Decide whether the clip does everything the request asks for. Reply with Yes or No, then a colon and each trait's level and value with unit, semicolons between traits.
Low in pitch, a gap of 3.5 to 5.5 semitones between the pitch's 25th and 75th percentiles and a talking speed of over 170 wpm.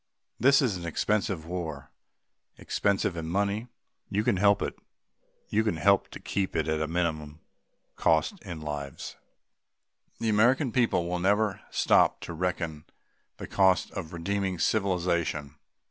No: very low, 90 Hz; average, 4.1 semitones; average, 140 wpm